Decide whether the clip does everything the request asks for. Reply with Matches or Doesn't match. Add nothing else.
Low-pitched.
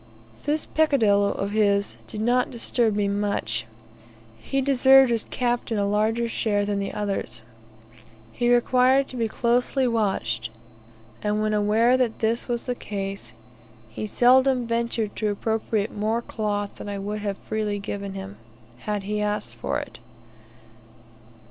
Doesn't match